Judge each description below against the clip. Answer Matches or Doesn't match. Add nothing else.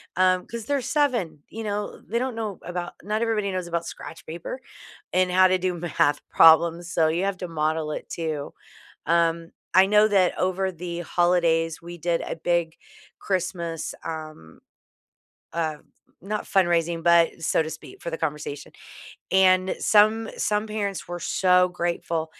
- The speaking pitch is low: Doesn't match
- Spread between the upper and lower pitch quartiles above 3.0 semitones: Doesn't match